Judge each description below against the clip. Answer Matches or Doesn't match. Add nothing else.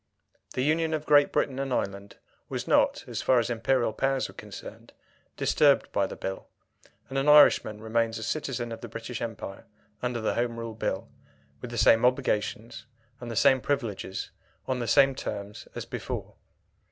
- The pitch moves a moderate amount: Matches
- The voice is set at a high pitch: Doesn't match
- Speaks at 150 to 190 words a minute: Matches